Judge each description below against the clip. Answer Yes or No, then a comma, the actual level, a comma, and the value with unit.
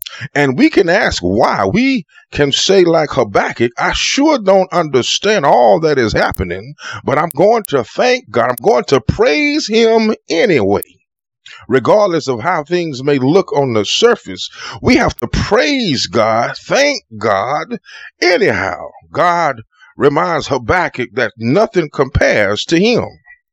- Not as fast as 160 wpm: Yes, average, 140 wpm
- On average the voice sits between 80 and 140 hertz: No, medium, 175 Hz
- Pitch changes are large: Yes, wide, 8.8 semitones